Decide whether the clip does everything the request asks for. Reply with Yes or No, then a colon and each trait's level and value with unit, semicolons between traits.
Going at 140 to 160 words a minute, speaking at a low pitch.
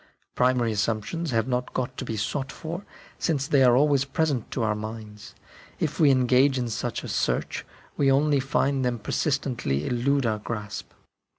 No: average, 170 wpm; low, 125 Hz